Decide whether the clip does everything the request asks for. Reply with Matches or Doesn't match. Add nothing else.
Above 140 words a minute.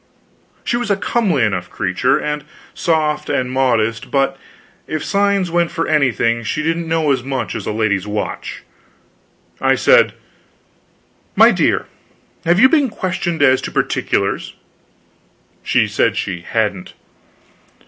Doesn't match